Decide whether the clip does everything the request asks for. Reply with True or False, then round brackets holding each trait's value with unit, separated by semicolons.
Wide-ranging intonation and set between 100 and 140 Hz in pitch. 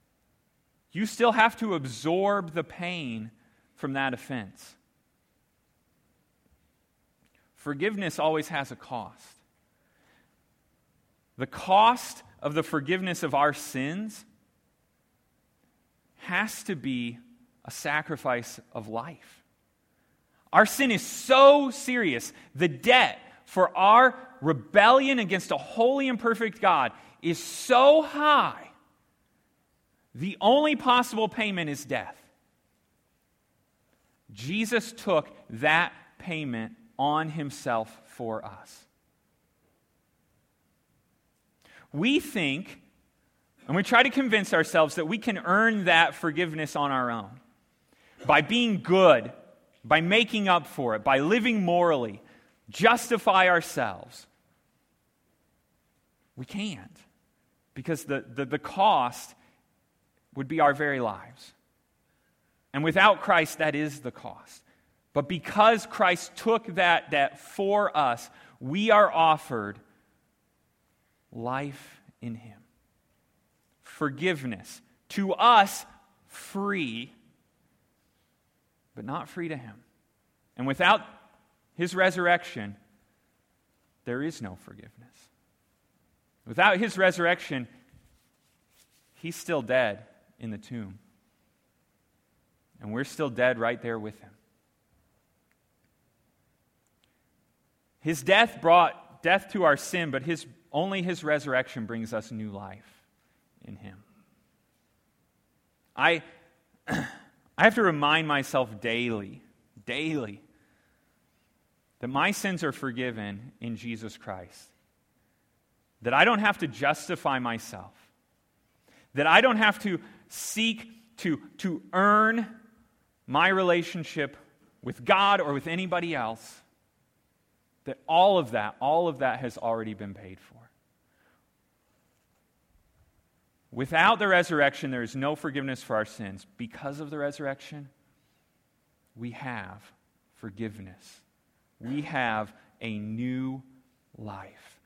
False (8.2 semitones; 150 Hz)